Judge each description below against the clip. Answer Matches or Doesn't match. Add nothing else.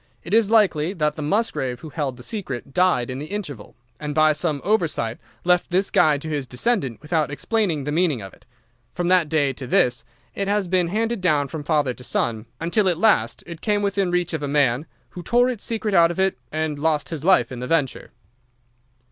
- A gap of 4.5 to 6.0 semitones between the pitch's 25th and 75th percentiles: Matches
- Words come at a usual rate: Doesn't match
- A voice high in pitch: Doesn't match